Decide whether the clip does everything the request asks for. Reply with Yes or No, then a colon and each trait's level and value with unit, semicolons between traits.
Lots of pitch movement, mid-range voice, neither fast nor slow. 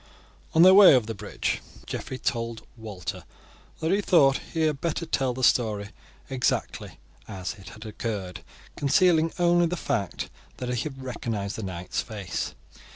No: wide, 7.3 semitones; low, 125 Hz; average, 160 wpm